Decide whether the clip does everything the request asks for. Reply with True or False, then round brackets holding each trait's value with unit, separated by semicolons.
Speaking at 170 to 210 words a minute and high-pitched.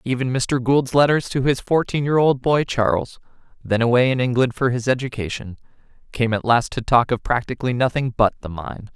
False (195 wpm; 125 Hz)